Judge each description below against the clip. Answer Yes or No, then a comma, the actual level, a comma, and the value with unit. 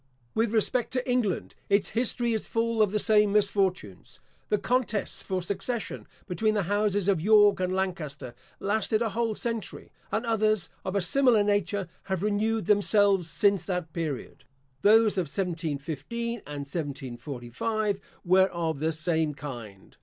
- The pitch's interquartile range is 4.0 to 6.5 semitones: Yes, average, 4.6 semitones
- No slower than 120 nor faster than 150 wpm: Yes, average, 145 wpm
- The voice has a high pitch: Yes, high, 200 Hz